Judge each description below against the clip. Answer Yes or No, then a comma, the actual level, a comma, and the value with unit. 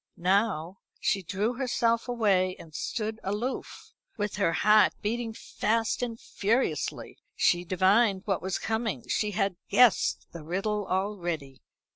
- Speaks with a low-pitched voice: No, high, 205 Hz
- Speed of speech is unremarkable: No, slow, 130 wpm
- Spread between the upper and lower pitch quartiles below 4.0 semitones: Yes, average, 3.4 semitones